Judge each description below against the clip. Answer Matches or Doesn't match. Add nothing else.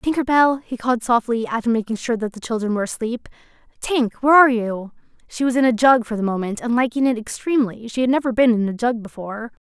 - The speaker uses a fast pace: Matches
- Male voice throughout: Doesn't match